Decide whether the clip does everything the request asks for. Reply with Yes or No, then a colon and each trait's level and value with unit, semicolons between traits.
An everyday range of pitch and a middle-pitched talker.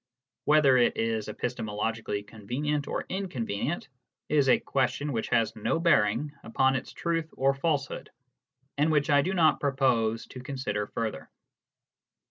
No: average, 4.7 semitones; low, 130 Hz